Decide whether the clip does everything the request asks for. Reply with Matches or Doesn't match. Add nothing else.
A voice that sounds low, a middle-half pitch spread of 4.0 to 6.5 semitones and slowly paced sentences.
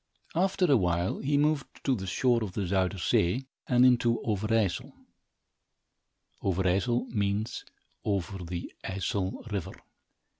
Matches